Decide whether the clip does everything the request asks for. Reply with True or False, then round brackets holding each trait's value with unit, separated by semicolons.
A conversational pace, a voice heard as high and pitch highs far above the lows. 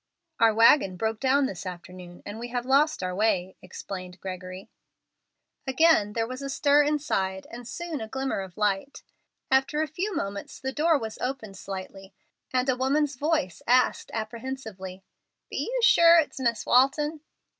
True (160 wpm; 240 Hz; 6.5 semitones)